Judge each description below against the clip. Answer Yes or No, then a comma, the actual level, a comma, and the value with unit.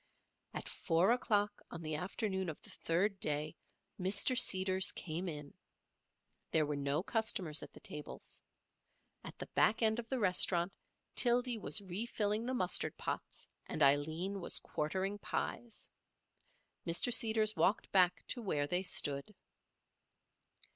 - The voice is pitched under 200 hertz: Yes, high, 190 Hz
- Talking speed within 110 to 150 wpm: Yes, slow, 135 wpm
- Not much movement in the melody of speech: No, average, 4.9 semitones